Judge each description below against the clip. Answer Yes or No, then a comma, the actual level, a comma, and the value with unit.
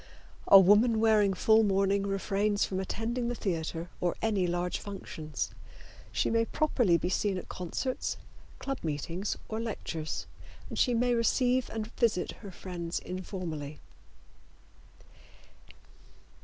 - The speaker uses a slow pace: Yes, slow, 125 wpm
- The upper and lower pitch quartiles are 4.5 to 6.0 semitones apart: No, average, 4.1 semitones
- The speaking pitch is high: Yes, high, 200 Hz